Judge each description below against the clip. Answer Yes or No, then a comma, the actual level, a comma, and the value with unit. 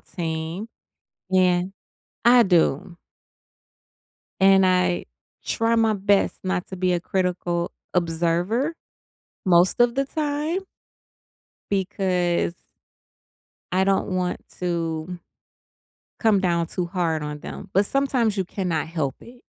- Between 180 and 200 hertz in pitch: Yes, medium, 185 Hz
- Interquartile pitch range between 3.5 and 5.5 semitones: No, average, 3.0 semitones